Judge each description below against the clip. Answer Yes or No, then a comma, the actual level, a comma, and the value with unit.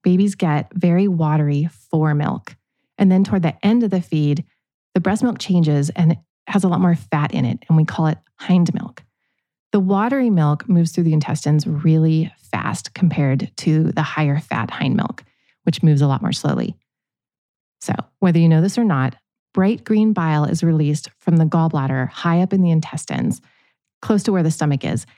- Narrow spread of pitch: No, average, 3.6 semitones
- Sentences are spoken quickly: No, average, 195 wpm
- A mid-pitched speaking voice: Yes, medium, 165 Hz